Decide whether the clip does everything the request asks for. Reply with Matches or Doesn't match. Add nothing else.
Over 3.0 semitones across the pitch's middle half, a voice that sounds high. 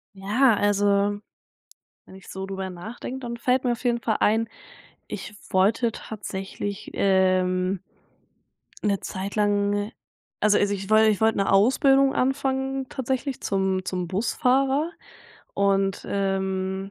Matches